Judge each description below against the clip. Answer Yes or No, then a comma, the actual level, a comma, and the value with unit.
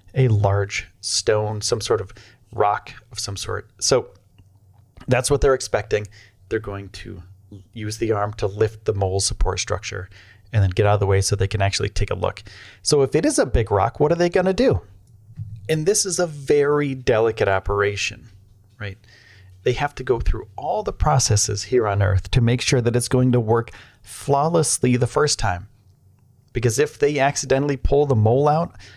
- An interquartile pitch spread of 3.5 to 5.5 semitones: Yes, average, 4.4 semitones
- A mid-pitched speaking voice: No, low, 110 Hz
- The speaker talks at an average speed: Yes, average, 195 wpm